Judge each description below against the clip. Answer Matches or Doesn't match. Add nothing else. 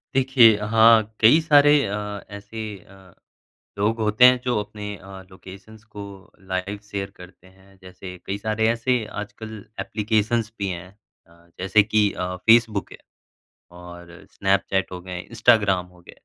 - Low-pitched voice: Matches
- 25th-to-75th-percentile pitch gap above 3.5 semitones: Doesn't match